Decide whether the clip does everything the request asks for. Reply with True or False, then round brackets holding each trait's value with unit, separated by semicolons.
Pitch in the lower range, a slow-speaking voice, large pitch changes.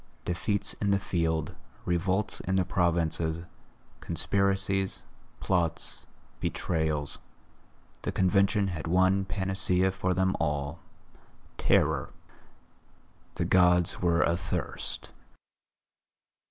False (90 Hz; 85 wpm; 2.5 semitones)